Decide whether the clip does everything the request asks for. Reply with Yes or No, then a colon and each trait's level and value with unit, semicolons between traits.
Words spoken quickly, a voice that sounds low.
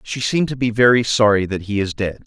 Yes: fast, 265 wpm; low, 110 Hz